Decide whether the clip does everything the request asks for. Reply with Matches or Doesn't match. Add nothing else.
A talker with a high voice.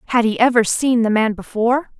Matches